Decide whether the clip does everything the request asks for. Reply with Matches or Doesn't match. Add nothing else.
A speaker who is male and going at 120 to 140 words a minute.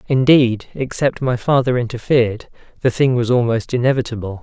Matches